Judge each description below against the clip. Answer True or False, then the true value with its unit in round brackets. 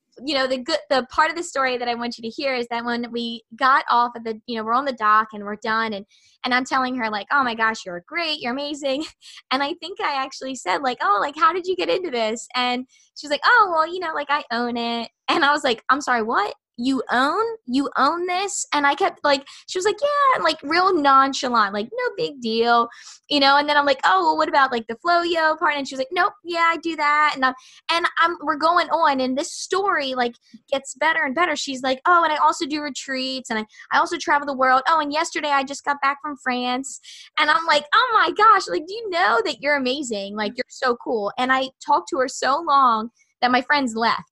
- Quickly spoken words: True (260 wpm)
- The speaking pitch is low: False (275 Hz)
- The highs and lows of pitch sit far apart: False (4.5 semitones)